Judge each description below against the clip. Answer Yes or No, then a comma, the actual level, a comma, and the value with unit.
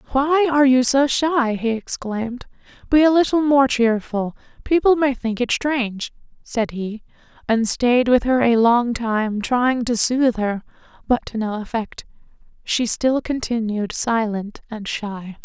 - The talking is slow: No, average, 150 wpm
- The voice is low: No, high, 245 Hz